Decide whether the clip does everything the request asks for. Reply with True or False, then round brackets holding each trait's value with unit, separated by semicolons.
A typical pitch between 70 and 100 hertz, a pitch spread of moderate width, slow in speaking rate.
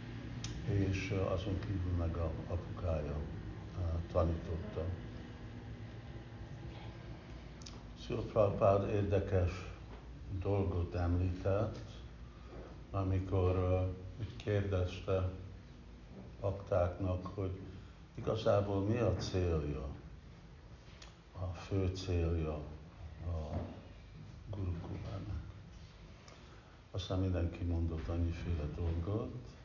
True (95 Hz; 3.0 semitones; 65 wpm)